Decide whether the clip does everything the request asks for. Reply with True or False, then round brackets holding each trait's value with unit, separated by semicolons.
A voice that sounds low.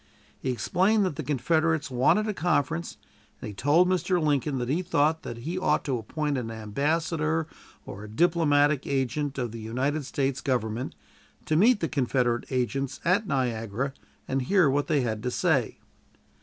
False (145 Hz)